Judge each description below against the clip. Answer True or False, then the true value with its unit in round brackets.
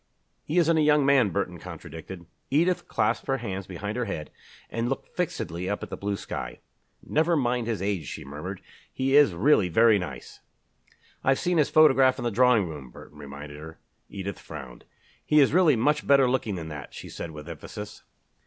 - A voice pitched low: True (105 Hz)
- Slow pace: False (190 wpm)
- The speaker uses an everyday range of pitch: False (8.2 semitones)